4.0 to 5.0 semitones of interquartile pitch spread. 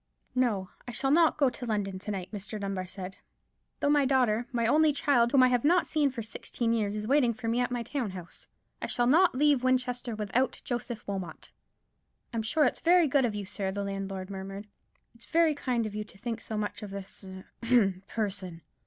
Yes: average, 4.4 semitones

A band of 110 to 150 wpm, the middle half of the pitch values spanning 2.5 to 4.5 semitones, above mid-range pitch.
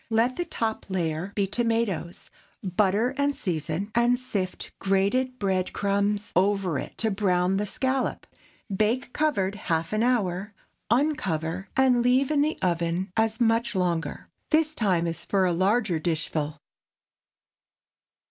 No: slow, 135 wpm; average, 4.9 semitones; high, 200 Hz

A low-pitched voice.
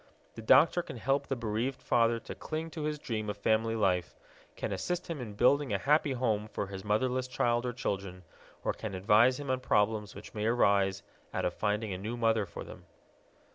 Yes: low, 115 Hz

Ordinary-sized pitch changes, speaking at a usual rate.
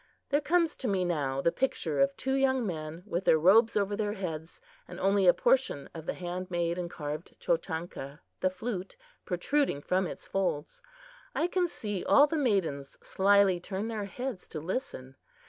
No: wide, 5.7 semitones; average, 180 wpm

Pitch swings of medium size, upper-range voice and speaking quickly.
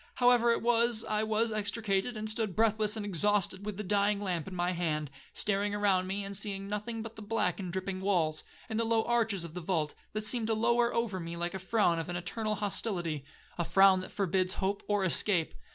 Yes: average, 3.0 semitones; high, 200 Hz; fast, 215 wpm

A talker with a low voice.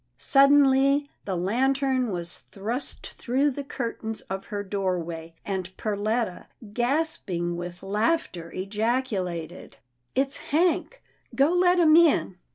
No: high, 225 Hz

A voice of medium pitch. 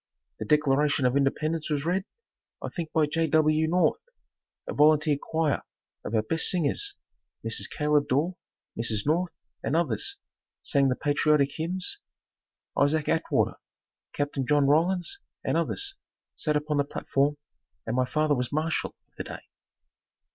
Yes: medium, 150 Hz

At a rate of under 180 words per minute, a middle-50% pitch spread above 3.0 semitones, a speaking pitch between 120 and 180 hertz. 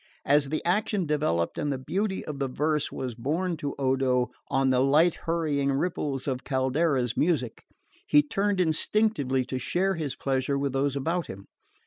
Yes: average, 165 wpm; average, 4.0 semitones; medium, 140 Hz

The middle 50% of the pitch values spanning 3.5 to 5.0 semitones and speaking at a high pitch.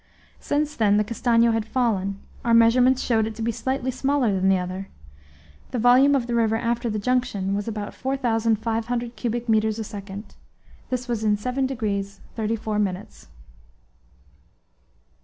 No: average, 2.7 semitones; high, 225 Hz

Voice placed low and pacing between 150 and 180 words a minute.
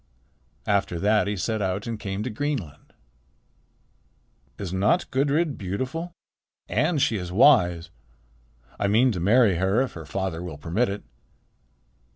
No: low, 100 Hz; average, 140 wpm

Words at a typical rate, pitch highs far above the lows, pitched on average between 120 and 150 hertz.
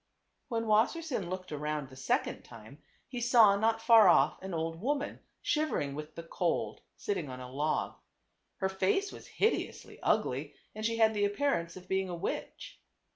No: average, 170 wpm; wide, 6.1 semitones; high, 190 Hz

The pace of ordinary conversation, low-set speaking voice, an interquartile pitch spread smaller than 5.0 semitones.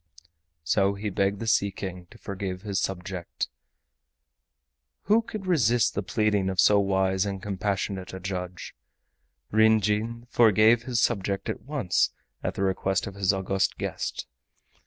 Yes: average, 145 wpm; low, 100 Hz; narrow, 2.4 semitones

